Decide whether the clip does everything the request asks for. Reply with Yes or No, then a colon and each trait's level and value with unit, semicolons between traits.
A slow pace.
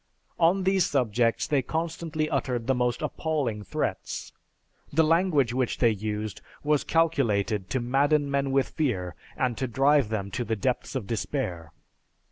No: average, 150 wpm